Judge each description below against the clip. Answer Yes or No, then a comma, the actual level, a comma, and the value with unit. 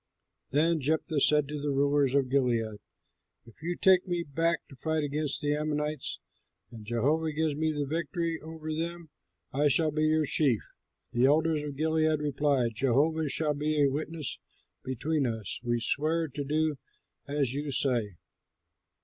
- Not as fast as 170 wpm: Yes, average, 160 wpm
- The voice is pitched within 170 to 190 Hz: No, medium, 150 Hz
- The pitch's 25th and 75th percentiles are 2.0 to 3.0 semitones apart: Yes, narrow, 2.6 semitones